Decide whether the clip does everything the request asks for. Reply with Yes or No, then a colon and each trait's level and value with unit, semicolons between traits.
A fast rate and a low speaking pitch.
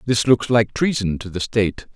Yes: fast, 215 wpm; low, 110 Hz